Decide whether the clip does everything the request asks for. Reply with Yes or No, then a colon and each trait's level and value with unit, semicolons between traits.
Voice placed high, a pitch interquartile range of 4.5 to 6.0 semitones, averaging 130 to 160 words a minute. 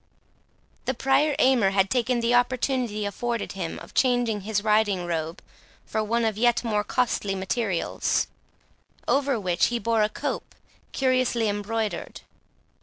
No: high, 225 Hz; average, 3.3 semitones; slow, 135 wpm